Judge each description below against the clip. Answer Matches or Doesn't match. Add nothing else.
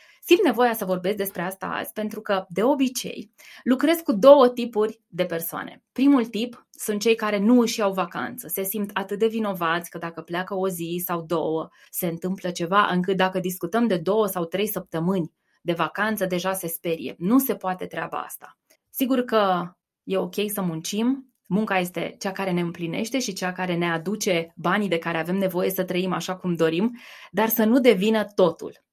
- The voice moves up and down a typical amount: Matches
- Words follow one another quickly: Matches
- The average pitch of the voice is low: Doesn't match